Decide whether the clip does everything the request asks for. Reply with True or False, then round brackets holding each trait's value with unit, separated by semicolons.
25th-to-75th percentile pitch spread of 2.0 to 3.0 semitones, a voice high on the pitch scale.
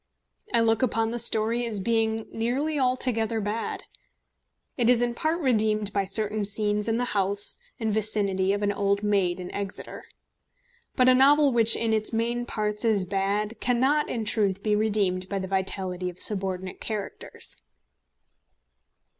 True (2.7 semitones; 215 Hz)